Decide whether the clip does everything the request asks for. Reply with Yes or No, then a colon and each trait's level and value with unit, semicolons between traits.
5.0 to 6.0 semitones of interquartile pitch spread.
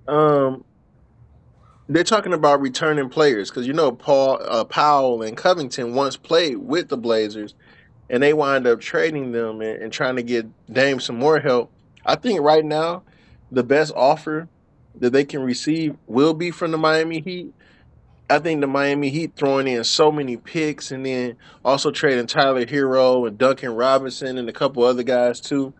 No: average, 3.7 semitones